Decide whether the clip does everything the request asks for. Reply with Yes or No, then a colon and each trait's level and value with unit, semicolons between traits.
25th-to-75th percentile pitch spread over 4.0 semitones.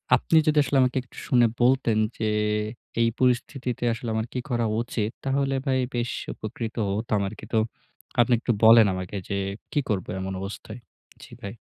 No: average, 2.8 semitones